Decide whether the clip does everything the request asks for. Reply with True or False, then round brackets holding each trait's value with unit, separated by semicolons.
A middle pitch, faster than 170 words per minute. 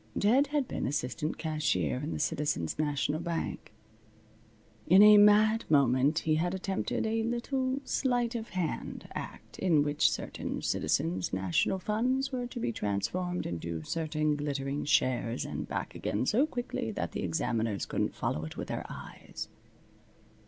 False (160 Hz; 150 wpm)